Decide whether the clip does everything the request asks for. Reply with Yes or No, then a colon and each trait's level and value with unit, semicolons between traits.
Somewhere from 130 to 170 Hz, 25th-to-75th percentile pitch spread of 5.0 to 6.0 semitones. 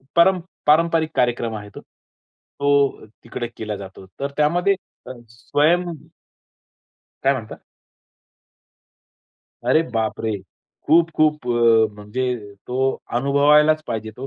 Yes: medium, 140 Hz; average, 5.3 semitones